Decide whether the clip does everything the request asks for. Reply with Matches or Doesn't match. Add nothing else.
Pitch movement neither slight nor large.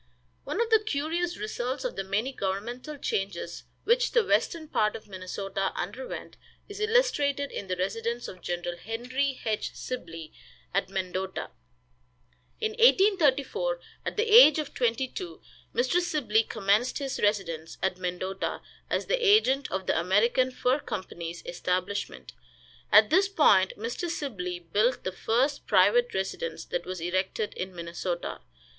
Doesn't match